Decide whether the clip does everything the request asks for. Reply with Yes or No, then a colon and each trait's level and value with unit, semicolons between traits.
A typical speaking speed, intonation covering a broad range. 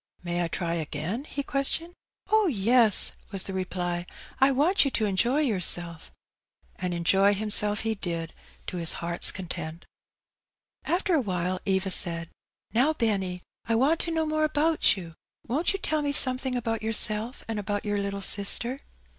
Yes: average, 165 wpm; wide, 7.0 semitones